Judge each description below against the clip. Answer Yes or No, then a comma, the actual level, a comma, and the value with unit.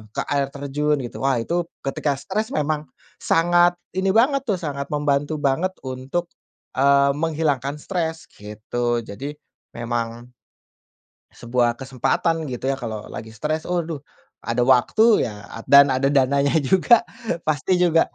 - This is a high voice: No, medium, 140 Hz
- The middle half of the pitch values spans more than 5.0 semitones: No, average, 4.2 semitones